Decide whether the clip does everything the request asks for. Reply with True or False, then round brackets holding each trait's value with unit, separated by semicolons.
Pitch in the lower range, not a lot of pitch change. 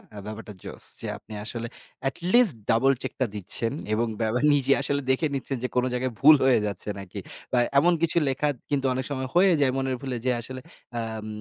False (130 Hz; 3.4 semitones)